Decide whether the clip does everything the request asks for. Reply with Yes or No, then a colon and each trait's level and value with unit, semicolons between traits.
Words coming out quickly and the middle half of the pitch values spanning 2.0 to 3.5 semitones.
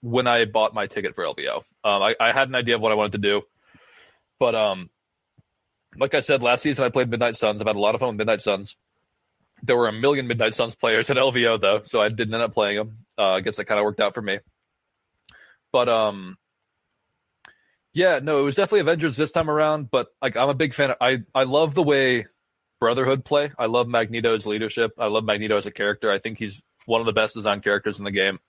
No: fast, 240 wpm; average, 3.9 semitones